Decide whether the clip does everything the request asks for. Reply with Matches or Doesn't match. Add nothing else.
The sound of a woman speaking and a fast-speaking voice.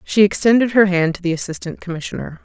Doesn't match